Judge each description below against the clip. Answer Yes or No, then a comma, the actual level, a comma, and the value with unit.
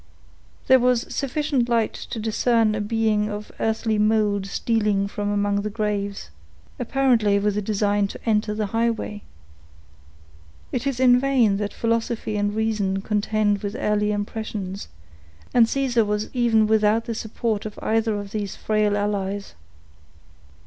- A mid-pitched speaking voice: No, high, 215 Hz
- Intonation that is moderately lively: No, narrow, 1.9 semitones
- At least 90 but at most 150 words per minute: Yes, average, 145 wpm